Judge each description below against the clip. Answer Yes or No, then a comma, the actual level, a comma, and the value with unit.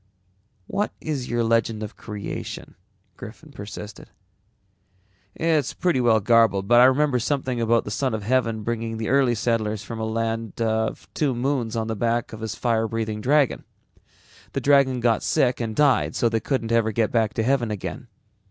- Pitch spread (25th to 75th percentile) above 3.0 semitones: No, narrow, 2.5 semitones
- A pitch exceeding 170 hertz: No, low, 115 Hz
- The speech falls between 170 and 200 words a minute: Yes, average, 175 wpm